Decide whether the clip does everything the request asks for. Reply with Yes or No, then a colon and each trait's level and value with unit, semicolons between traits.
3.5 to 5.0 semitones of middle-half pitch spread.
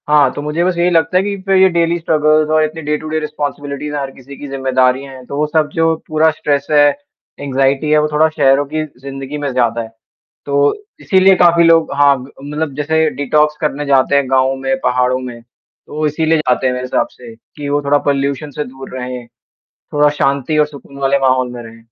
No: narrow, 2.6 semitones